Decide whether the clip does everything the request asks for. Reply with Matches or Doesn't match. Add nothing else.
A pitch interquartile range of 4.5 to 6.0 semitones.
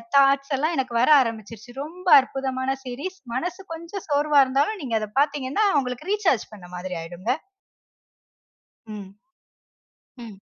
Matches